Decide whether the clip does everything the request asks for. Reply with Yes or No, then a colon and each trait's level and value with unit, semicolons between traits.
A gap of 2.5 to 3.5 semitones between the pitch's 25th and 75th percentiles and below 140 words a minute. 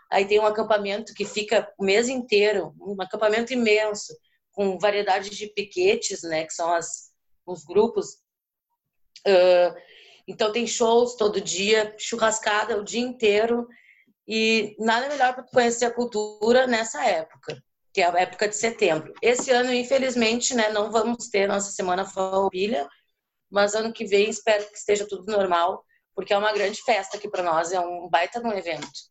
No: average, 2.9 semitones; average, 165 wpm